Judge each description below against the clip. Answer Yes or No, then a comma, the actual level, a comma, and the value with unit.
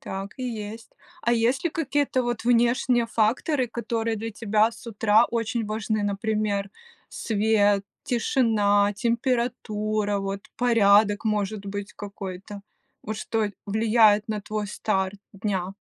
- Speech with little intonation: Yes, narrow, 2.3 semitones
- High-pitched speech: Yes, high, 215 Hz